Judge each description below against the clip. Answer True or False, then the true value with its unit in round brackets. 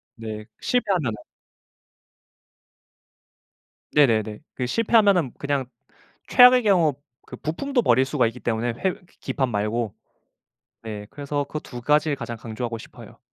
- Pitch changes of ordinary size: False (5.9 semitones)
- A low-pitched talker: True (130 Hz)